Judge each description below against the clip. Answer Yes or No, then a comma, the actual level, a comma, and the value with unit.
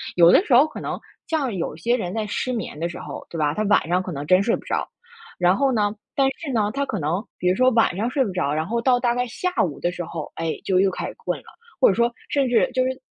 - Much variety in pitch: Yes, wide, 6.2 semitones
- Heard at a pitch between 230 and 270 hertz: No, high, 215 Hz